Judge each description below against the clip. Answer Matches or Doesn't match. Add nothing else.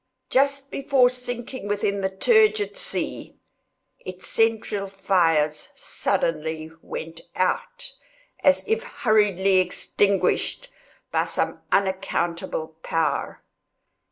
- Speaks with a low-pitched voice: Doesn't match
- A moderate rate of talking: Doesn't match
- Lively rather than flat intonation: Matches